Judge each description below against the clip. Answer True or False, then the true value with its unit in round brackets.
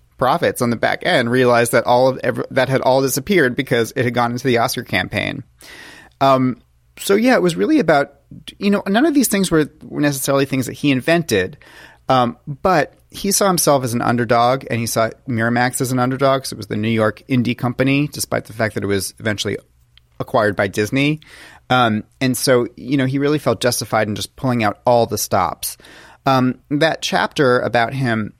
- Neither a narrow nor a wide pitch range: True (3.1 semitones)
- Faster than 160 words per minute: True (200 wpm)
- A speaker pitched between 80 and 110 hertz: False (125 Hz)